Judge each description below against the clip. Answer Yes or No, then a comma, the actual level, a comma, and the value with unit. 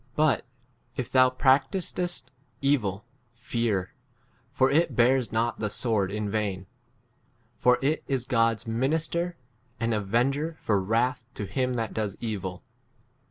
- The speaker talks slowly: Yes, slow, 130 wpm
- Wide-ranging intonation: No, average, 3.9 semitones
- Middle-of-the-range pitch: No, low, 120 Hz